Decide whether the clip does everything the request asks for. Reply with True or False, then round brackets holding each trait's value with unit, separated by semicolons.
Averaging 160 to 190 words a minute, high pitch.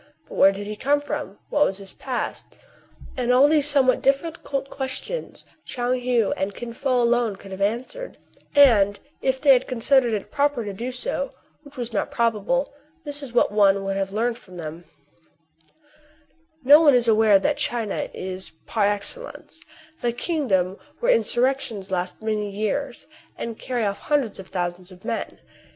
True (175 wpm; 240 Hz)